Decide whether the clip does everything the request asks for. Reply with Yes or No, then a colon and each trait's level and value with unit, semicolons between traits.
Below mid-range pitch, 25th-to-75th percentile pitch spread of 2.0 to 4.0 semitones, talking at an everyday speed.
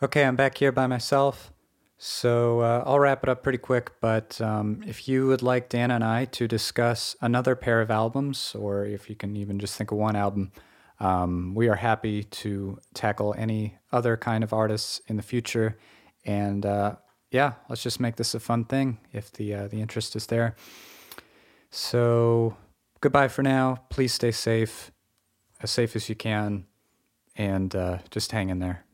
Yes: low, 110 Hz; average, 2.8 semitones; average, 180 wpm